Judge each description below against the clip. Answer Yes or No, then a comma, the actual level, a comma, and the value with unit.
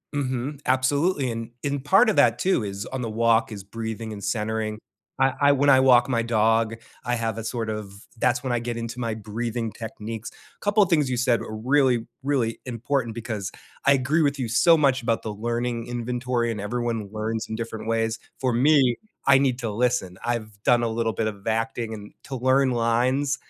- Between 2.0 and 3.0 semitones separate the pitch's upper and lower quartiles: Yes, average, 2.7 semitones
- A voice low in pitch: Yes, low, 120 Hz